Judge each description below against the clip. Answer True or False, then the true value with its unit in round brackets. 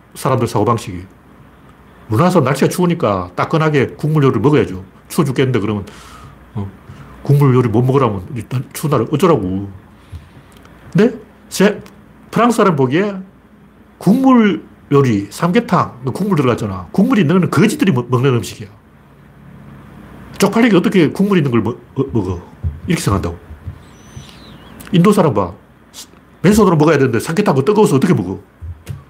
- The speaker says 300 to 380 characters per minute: True (320 characters per minute)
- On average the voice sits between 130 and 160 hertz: True (135 Hz)